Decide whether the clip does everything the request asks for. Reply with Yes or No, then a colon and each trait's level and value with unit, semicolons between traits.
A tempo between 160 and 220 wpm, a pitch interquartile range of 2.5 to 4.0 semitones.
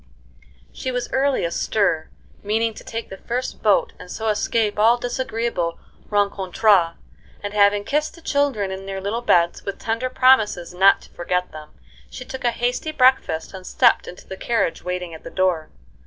No: average, 170 wpm; average, 4.7 semitones